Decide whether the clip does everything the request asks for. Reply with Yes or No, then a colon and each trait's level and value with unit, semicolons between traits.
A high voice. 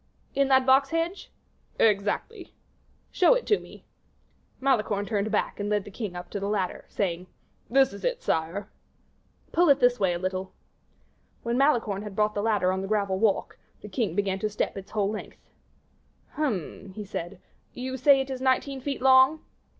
Yes: high, 215 Hz